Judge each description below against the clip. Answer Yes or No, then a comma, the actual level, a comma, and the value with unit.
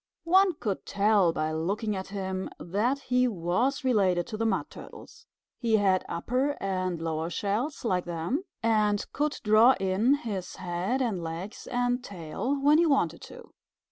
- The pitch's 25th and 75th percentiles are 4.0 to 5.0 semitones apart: No, wide, 5.5 semitones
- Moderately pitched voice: No, high, 205 Hz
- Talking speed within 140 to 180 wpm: Yes, average, 160 wpm